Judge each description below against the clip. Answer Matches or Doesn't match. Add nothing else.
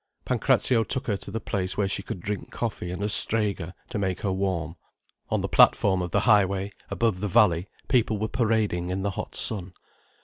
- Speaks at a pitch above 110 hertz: Doesn't match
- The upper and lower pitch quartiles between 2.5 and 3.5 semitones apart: Matches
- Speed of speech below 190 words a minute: Doesn't match